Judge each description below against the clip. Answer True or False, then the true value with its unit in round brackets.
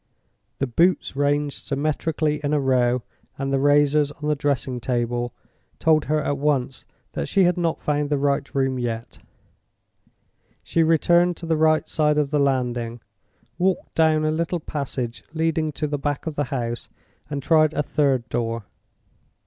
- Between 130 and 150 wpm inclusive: False (165 wpm)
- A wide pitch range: False (2.9 semitones)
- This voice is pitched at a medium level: True (145 Hz)